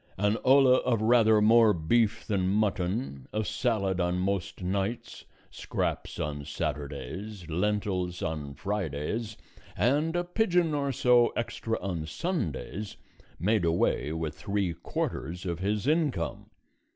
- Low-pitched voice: Yes, low, 100 Hz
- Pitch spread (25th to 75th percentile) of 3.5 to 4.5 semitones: No, average, 5.3 semitones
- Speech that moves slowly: Yes, slow, 125 wpm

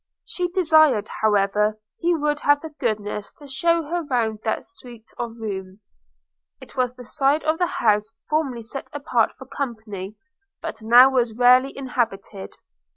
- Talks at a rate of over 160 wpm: No, average, 155 wpm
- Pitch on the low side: No, high, 245 Hz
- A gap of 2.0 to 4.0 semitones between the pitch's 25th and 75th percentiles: No, average, 5.3 semitones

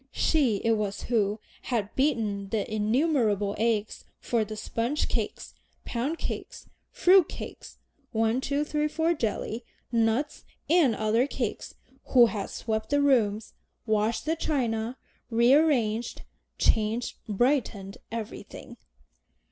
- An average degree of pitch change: Yes, average, 4.6 semitones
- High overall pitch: Yes, high, 230 Hz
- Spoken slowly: Yes, slow, 115 wpm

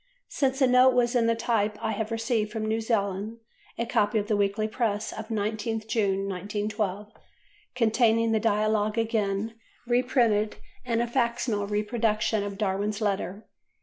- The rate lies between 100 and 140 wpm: No, average, 150 wpm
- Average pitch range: No, narrow, 1.9 semitones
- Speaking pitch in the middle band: No, high, 220 Hz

